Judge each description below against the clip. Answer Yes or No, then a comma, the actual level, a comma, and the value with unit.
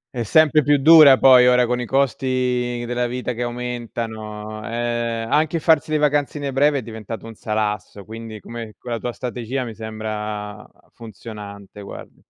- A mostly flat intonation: No, average, 3.0 semitones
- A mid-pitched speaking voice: No, low, 120 Hz